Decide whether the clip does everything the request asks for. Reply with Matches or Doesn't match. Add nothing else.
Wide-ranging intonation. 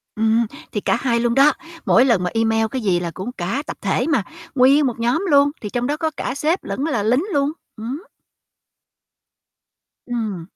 Doesn't match